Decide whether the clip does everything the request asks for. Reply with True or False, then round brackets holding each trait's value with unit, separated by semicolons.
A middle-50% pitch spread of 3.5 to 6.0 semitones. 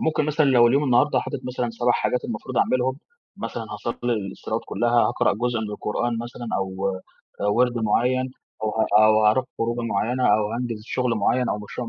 False (2.6 semitones)